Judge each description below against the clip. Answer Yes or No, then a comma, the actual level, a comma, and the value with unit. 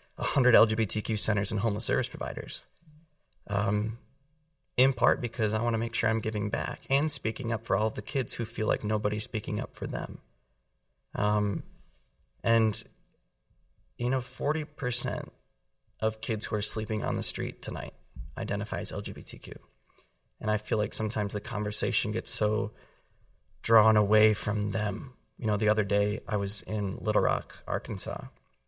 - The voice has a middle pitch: No, low, 110 Hz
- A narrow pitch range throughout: Yes, narrow, 2.0 semitones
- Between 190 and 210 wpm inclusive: No, average, 155 wpm